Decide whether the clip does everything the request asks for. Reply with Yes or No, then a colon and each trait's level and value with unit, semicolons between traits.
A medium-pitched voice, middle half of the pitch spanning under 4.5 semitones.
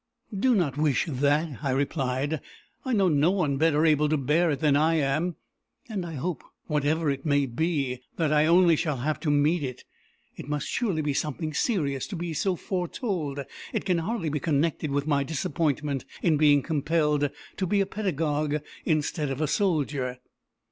Yes: medium, 150 Hz; average, 2.9 semitones